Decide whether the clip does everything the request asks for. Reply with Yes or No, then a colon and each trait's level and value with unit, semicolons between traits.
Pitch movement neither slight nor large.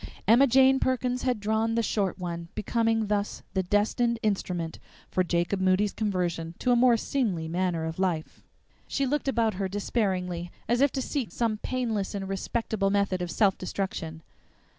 Yes: average, 4.3 semitones